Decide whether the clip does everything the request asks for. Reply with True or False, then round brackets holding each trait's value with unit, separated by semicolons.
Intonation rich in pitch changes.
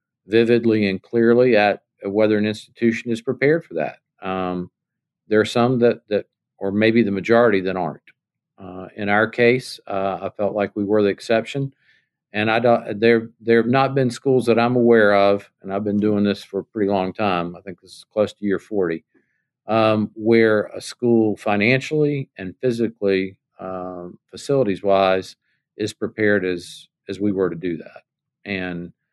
False (3.2 semitones)